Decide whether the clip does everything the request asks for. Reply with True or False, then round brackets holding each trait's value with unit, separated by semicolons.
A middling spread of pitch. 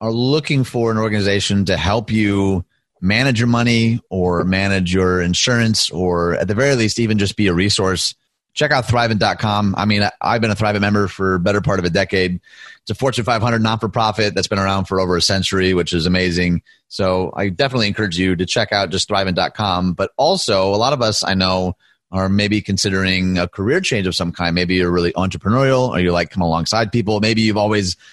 True (3.1 semitones)